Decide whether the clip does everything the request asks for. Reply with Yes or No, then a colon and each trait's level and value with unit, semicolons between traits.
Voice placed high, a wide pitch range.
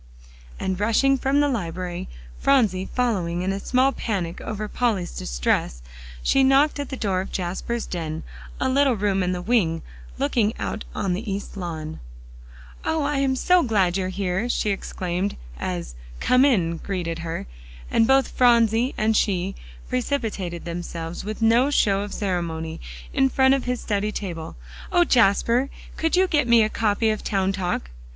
Yes: high, 205 Hz; wide, 5.8 semitones